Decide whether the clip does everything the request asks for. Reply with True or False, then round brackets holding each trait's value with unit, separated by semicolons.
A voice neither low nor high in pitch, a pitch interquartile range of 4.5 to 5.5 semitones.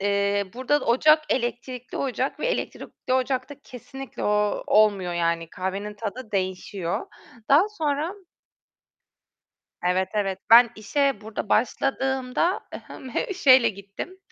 False (235 Hz; 5.1 semitones)